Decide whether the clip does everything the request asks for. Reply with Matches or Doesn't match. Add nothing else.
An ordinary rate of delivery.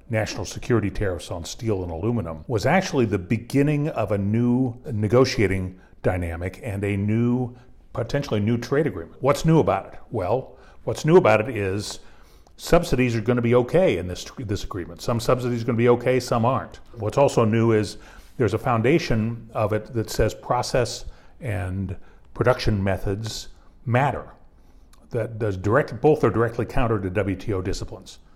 Matches